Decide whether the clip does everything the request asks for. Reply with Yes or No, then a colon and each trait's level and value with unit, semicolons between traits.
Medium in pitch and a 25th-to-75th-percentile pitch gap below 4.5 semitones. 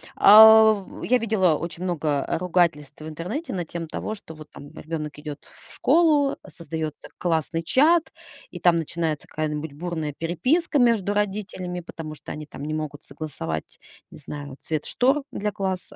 No: medium, 170 Hz; average, 5.3 semitones